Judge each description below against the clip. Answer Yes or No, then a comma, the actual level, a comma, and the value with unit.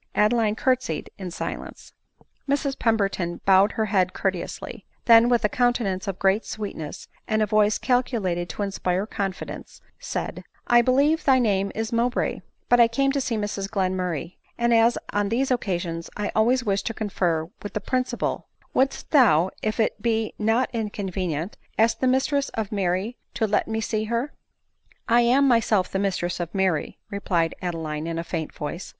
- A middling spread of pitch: Yes, average, 4.1 semitones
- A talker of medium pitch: No, high, 210 Hz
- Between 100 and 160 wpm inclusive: No, average, 175 wpm